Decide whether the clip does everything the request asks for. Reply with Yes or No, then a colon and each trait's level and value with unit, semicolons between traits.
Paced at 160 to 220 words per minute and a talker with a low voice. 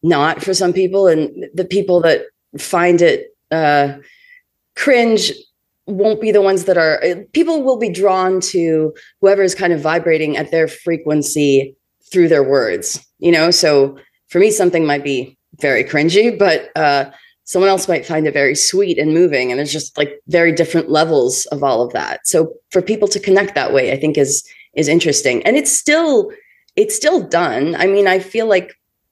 No: average, 185 wpm; medium, 175 Hz